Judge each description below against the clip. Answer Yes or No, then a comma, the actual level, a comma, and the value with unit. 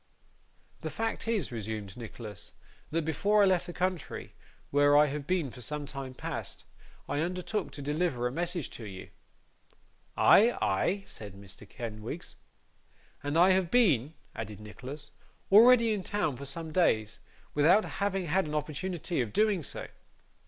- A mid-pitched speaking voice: Yes, medium, 150 Hz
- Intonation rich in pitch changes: Yes, wide, 7.1 semitones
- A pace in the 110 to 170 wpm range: Yes, average, 150 wpm